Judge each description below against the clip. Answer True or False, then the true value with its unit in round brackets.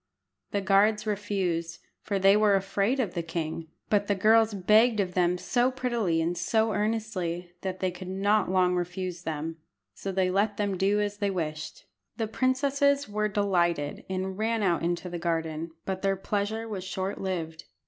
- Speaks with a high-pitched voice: True (195 Hz)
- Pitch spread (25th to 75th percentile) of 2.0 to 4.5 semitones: True (3.2 semitones)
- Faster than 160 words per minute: True (175 wpm)